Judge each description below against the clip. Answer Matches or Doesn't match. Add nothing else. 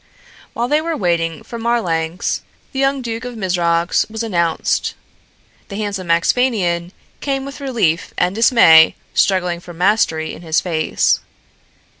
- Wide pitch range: Matches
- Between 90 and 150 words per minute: Matches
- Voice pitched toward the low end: Doesn't match